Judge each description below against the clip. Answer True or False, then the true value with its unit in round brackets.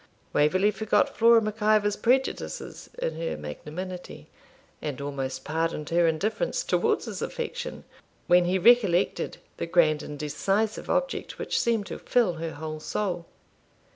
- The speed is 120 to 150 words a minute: True (140 wpm)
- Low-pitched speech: False (180 Hz)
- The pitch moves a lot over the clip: True (5.9 semitones)